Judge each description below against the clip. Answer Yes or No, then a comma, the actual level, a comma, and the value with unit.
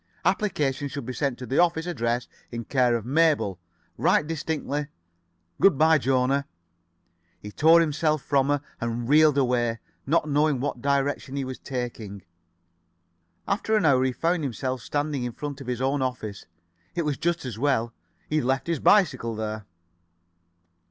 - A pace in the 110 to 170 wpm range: Yes, average, 165 wpm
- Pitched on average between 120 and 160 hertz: Yes, medium, 140 Hz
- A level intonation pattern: No, average, 3.7 semitones